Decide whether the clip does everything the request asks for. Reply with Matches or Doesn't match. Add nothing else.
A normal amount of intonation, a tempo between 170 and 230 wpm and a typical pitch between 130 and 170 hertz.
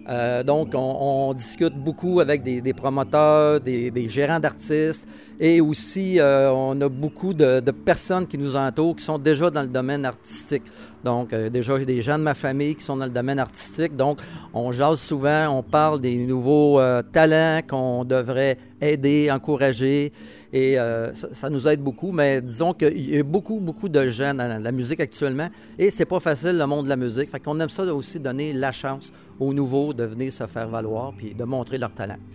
Matches